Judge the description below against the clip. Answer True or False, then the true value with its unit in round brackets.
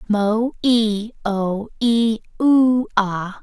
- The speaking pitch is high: True (220 Hz)